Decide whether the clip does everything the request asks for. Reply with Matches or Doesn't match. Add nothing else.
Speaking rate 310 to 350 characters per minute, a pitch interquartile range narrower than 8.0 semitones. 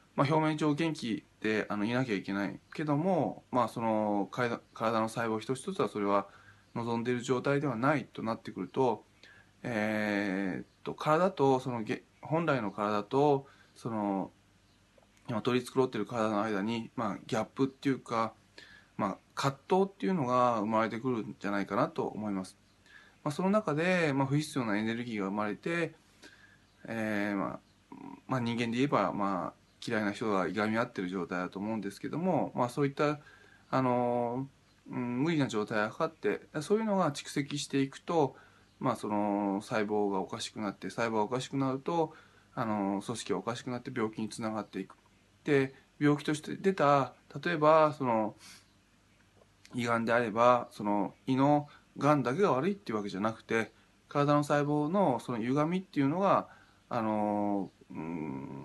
Matches